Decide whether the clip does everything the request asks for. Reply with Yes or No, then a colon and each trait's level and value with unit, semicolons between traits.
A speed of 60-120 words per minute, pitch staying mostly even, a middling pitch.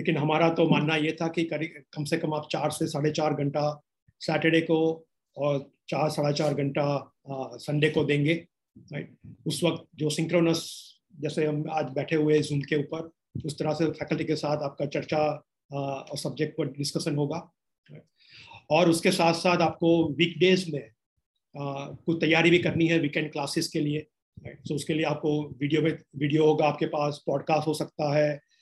No: average, 175 wpm; narrow, 1.6 semitones; medium, 155 Hz